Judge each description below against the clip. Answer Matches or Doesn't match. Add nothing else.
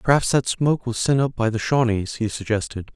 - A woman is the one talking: Doesn't match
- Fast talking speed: Matches